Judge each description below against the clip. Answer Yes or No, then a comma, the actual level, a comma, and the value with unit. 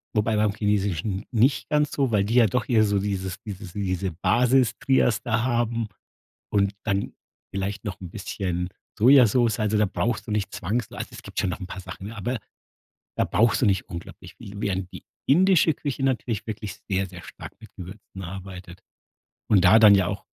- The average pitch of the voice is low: Yes, low, 105 Hz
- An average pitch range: Yes, average, 3.5 semitones